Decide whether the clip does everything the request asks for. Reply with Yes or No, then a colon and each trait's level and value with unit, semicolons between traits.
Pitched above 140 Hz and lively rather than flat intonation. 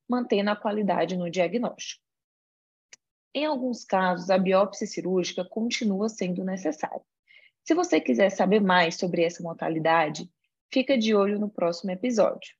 No: high, 190 Hz; average, 3.8 semitones